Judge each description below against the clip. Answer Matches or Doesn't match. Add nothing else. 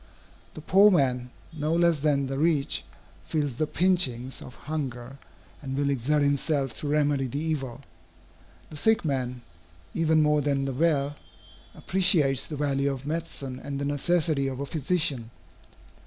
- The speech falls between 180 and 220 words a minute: Doesn't match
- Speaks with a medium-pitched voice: Matches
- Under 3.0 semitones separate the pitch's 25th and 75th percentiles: Matches